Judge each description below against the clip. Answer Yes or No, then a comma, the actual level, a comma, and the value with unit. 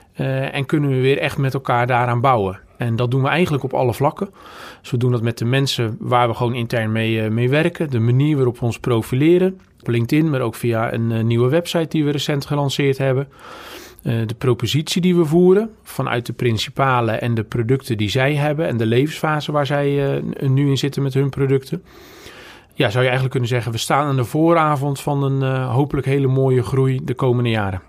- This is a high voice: No, low, 135 Hz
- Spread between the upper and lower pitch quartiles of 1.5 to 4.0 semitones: Yes, average, 3.3 semitones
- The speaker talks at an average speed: No, fast, 215 wpm